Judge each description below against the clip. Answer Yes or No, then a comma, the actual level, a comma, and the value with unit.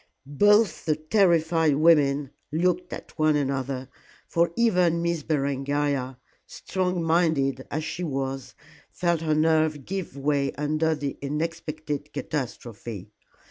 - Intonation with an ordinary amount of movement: Yes, average, 3.3 semitones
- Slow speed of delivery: Yes, slow, 115 wpm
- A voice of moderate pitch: Yes, medium, 155 Hz